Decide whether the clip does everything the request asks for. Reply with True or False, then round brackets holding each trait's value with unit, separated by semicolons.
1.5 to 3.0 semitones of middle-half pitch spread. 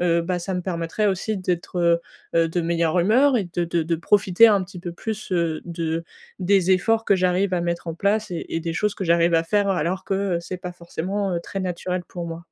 True (2.4 semitones)